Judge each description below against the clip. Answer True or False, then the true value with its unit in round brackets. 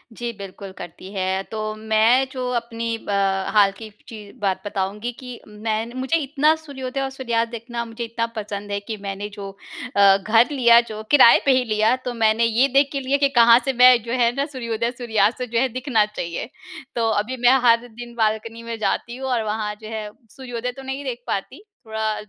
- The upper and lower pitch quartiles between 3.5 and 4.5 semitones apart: False (2.8 semitones)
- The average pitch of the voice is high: True (230 Hz)